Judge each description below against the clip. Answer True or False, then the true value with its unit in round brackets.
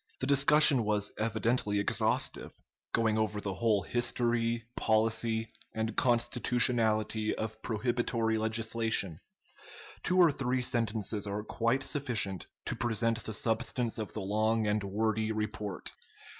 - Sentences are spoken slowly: True (120 wpm)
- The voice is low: True (110 Hz)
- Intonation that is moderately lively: False (1.8 semitones)